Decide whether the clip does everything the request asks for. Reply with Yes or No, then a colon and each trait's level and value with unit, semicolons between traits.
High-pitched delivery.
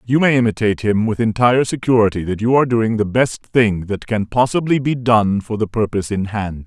No: low, 110 Hz